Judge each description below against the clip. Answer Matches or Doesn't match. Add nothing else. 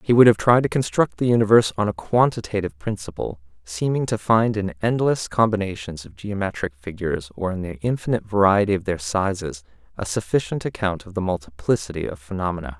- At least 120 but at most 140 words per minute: Doesn't match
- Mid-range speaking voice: Doesn't match